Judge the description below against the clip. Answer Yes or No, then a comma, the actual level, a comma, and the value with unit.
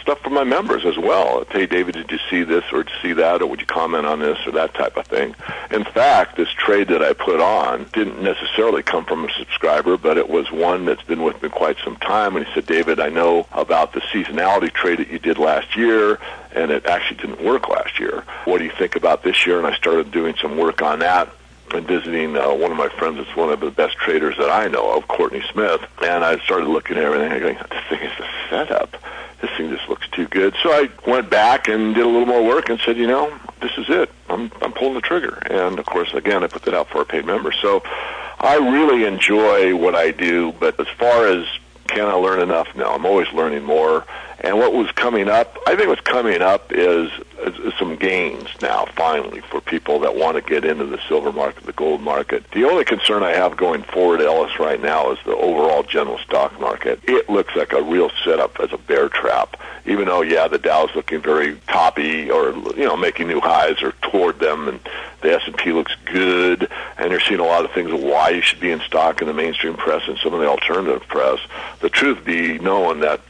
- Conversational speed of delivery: No, fast, 235 wpm